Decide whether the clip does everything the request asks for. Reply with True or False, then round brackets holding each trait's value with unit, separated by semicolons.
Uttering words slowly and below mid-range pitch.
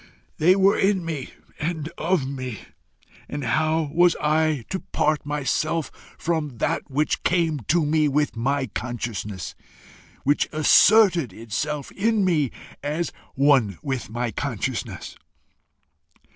False (120 wpm; 150 Hz)